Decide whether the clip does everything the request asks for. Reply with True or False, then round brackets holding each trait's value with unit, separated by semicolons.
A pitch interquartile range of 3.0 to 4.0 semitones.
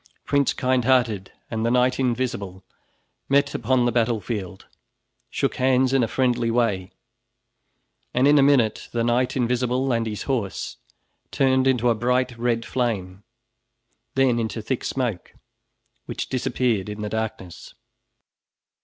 False (2.6 semitones)